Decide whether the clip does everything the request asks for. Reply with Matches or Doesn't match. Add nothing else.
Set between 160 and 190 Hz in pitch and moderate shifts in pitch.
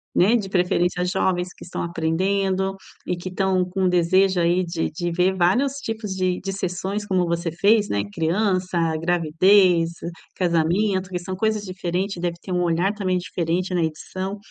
Doesn't match